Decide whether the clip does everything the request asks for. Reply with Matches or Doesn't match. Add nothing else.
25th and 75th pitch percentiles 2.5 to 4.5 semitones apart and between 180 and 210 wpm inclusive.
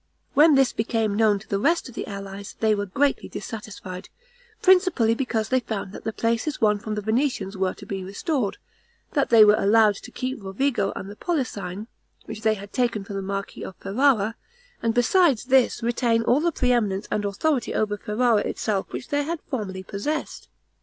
Matches